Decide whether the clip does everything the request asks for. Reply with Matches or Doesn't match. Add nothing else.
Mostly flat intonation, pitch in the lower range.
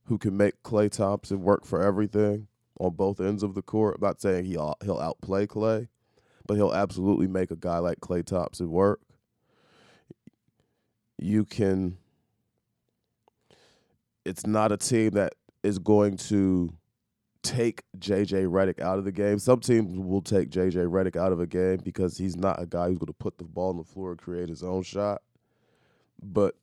Matches